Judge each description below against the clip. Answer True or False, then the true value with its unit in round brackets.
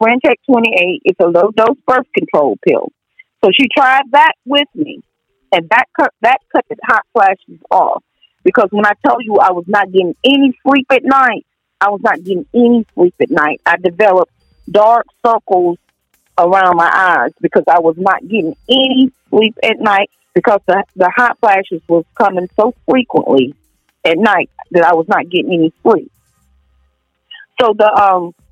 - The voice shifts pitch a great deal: True (6.4 semitones)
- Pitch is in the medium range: False (210 Hz)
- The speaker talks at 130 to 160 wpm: False (175 wpm)